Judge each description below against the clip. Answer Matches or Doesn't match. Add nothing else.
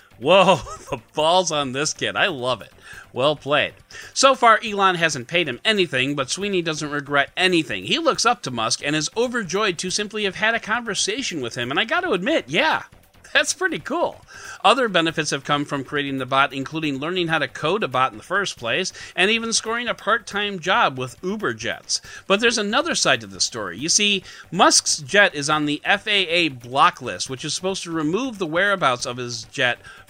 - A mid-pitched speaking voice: Matches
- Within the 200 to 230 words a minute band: Matches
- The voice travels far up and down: Matches